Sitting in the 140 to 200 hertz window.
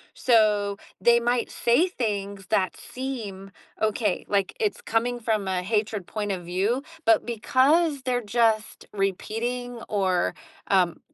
No: high, 220 Hz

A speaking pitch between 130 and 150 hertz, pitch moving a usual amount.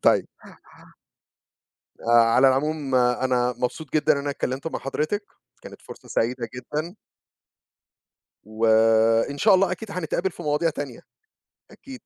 Yes: medium, 140 Hz; average, 4.5 semitones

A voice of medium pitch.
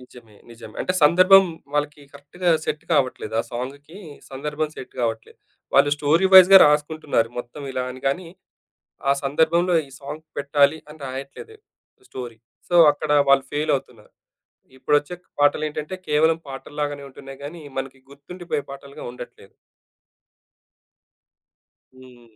Yes: medium, 145 Hz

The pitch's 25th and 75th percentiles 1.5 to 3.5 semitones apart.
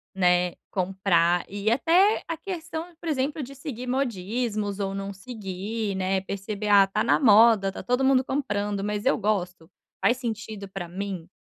No: average, 4.7 semitones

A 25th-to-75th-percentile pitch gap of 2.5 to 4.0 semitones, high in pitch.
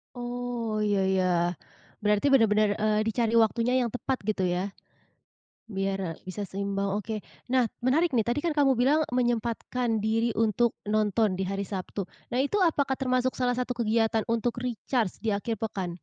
Yes: average, 3.1 semitones; high, 225 Hz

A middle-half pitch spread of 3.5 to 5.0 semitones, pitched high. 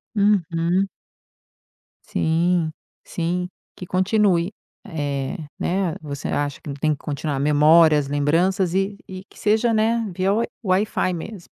No: average, 4.3 semitones; medium, 175 Hz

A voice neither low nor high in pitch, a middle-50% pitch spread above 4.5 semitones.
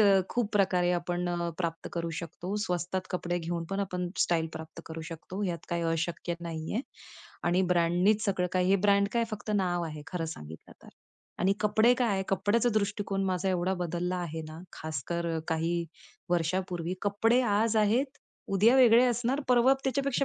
No: medium, 180 Hz; average, 3.3 semitones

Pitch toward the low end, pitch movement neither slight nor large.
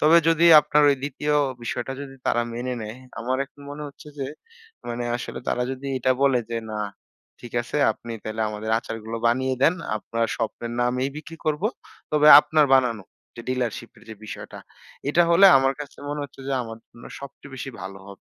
Yes: low, 130 Hz; average, 3.7 semitones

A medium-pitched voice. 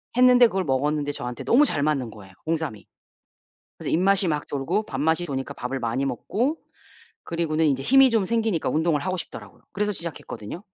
Yes: medium, 160 Hz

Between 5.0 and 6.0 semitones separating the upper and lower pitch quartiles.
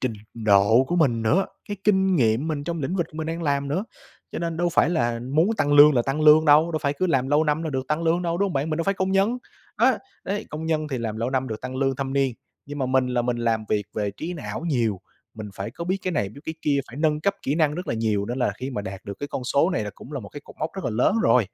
Yes: average, 5.3 semitones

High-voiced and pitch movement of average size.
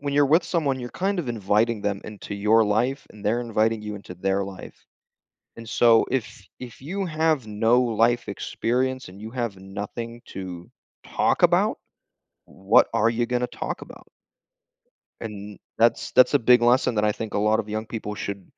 No: low, 115 Hz; average, 3.1 semitones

